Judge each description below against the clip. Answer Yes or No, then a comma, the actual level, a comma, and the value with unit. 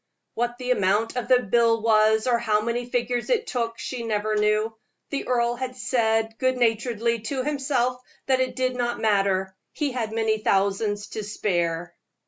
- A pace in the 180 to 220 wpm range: No, average, 170 wpm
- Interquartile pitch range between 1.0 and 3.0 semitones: Yes, average, 2.7 semitones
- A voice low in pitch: No, high, 230 Hz